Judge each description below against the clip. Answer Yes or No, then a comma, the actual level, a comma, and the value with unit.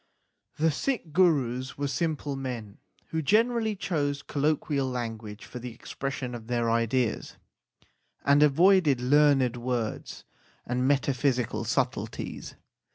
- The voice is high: No, low, 135 Hz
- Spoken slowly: Yes, slow, 115 wpm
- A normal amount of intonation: Yes, average, 3.6 semitones